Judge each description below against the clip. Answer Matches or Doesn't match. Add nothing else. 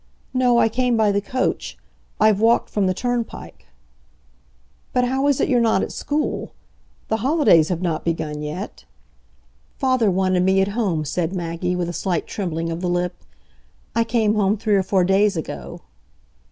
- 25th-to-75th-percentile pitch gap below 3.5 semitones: Doesn't match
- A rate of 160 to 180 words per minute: Matches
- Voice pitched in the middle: Doesn't match